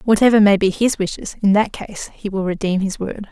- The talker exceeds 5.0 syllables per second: Yes, 5.5 syllables/s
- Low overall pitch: No, high, 200 Hz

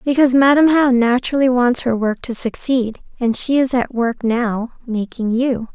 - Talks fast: No, average, 180 wpm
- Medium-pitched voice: No, high, 245 Hz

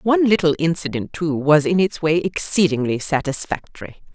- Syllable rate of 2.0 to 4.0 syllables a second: No, 5.2 syllables/s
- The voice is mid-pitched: Yes, medium, 160 Hz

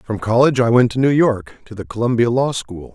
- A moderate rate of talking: No, fast, 245 wpm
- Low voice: Yes, low, 115 Hz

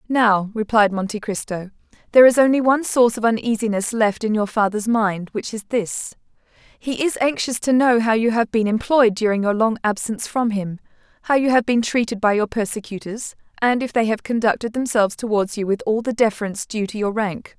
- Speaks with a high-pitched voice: Yes, high, 220 Hz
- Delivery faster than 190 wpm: Yes, average, 200 wpm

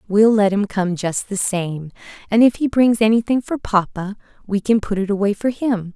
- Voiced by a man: No, female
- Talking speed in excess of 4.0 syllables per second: Yes, 5.0 syllables/s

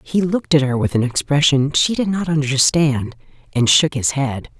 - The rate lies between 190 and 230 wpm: Yes, average, 195 wpm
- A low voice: No, medium, 145 Hz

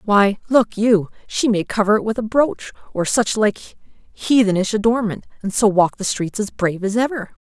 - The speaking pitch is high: Yes, high, 210 Hz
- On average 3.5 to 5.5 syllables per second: Yes, 4.9 syllables/s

